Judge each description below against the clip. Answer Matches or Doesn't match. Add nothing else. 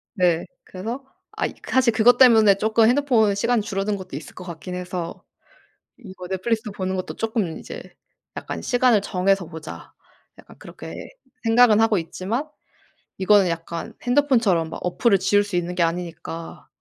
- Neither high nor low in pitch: Doesn't match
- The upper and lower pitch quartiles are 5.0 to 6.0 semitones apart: Doesn't match